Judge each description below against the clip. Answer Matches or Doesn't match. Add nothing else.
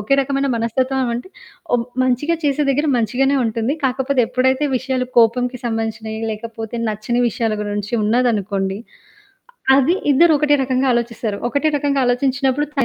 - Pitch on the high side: Matches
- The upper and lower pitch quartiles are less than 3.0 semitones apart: Doesn't match